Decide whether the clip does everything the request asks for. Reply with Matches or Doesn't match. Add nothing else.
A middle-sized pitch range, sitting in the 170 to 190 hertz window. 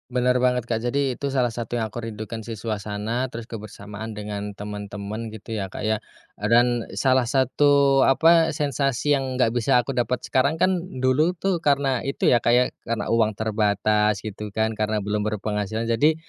Doesn't match